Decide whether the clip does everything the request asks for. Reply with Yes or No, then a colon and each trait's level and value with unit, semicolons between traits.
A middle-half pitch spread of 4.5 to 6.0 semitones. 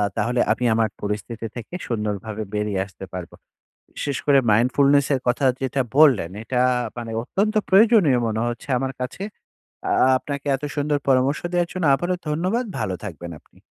Yes: average, 5.2 semitones